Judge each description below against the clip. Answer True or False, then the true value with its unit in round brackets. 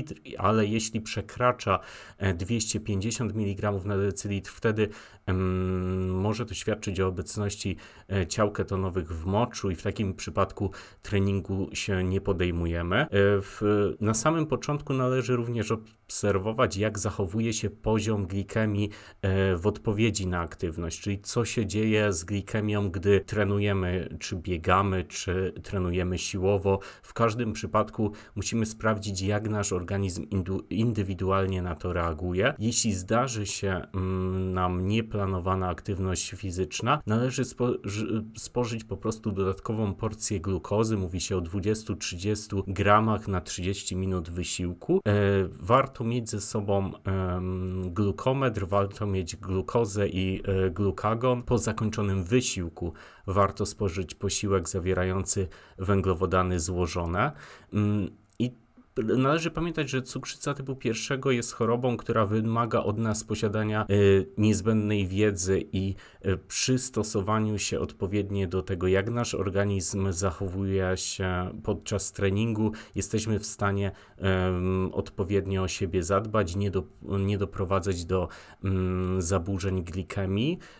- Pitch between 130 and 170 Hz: False (100 Hz)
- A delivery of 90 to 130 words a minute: True (115 wpm)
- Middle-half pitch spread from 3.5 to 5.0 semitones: False (2.6 semitones)